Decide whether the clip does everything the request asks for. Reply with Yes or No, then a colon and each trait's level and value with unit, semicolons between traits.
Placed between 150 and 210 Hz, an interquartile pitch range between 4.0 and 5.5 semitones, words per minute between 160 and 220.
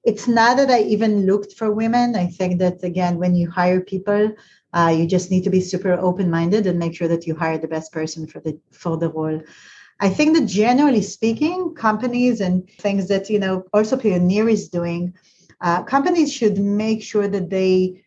No: high, 190 Hz; average, 3.5 semitones; average, 200 wpm